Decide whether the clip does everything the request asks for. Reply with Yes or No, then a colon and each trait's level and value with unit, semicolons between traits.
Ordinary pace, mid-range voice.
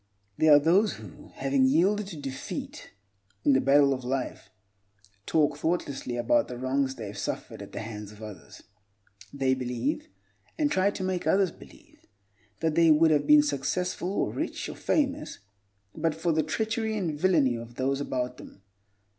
Yes: average, 165 wpm; medium, 145 Hz